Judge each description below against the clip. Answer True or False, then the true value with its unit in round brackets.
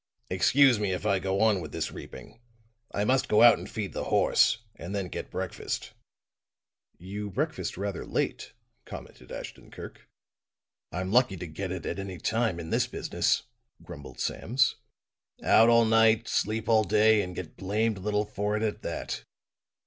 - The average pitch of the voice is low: True (105 Hz)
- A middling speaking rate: True (165 wpm)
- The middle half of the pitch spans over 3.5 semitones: False (2.9 semitones)